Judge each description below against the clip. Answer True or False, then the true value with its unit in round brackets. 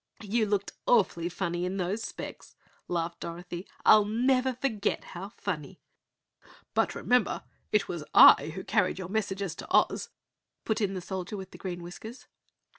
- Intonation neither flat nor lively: True (3.5 semitones)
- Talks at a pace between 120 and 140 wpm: False (150 wpm)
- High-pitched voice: True (195 Hz)